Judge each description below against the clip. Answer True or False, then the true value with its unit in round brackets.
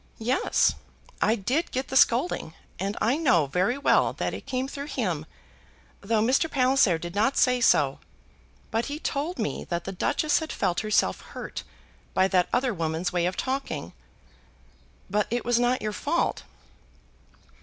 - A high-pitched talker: True (235 Hz)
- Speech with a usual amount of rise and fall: False (6.2 semitones)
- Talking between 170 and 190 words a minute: False (160 wpm)